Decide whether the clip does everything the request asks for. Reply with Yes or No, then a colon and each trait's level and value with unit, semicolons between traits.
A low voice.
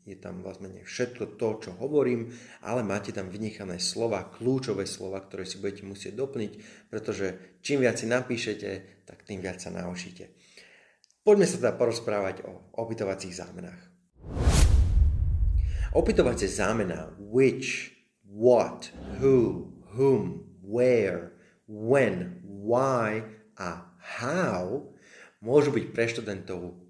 Yes: low, 105 Hz